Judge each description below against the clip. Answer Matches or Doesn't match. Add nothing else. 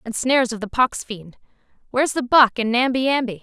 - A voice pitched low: Doesn't match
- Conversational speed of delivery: Matches